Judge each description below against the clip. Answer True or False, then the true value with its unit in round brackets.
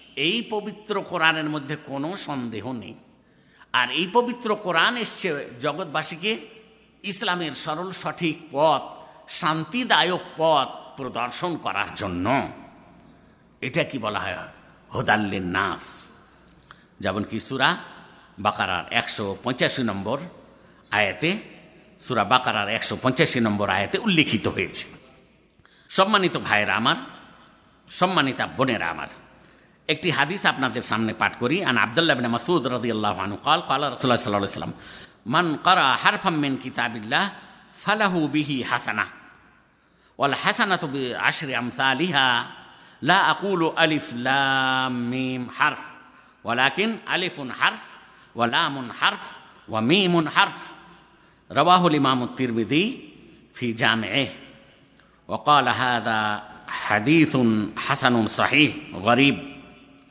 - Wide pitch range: True (6.5 semitones)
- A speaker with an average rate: True (105 wpm)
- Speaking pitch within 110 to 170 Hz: True (140 Hz)